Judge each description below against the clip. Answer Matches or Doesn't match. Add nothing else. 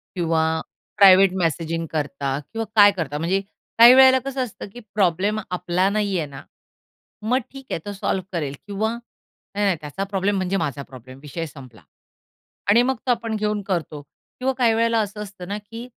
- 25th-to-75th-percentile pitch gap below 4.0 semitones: Doesn't match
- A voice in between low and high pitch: Doesn't match